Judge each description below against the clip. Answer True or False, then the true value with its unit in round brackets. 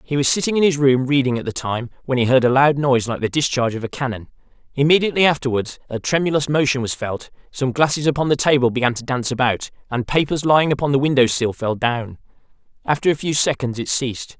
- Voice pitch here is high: False (135 Hz)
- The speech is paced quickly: True (220 wpm)